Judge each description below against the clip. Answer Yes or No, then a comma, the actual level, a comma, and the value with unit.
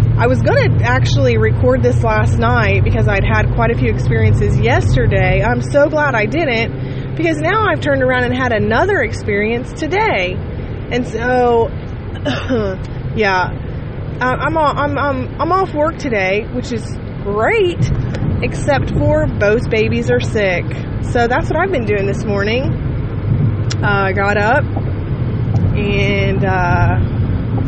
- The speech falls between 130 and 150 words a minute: Yes, average, 140 wpm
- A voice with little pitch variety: Yes, narrow, 2.3 semitones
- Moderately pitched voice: No, low, 120 Hz